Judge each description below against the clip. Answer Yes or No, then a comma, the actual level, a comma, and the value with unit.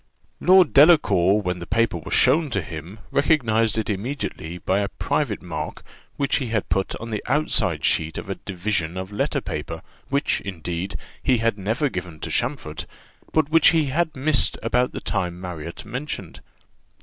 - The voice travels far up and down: Yes, wide, 7.2 semitones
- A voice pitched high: No, low, 105 Hz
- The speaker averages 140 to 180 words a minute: Yes, average, 170 wpm